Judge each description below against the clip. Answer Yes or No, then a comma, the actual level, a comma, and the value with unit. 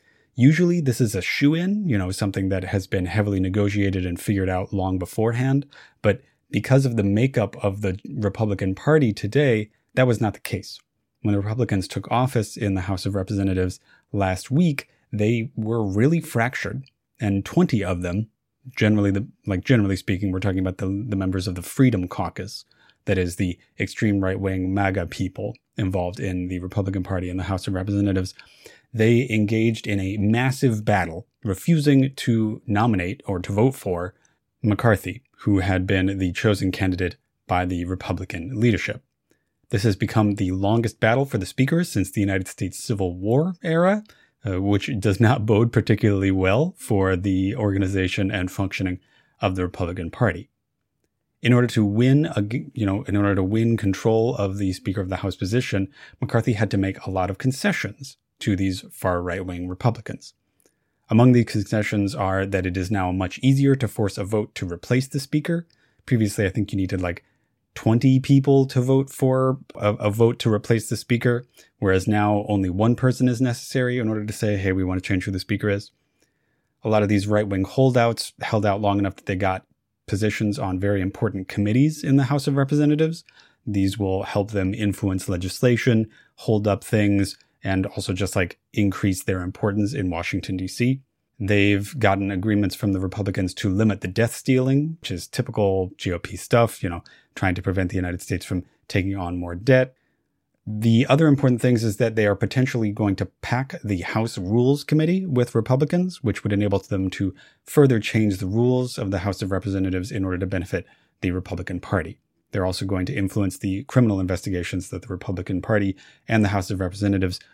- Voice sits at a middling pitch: No, low, 105 Hz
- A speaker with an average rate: Yes, average, 185 wpm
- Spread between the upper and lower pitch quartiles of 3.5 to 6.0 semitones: Yes, average, 4.1 semitones